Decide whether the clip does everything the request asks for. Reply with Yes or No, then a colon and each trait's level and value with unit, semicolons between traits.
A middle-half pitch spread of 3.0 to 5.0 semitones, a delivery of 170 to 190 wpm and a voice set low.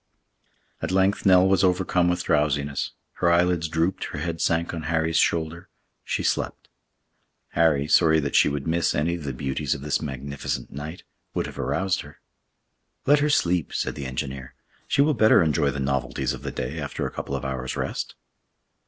Yes: average, 3.9 semitones; average, 180 wpm; very low, 80 Hz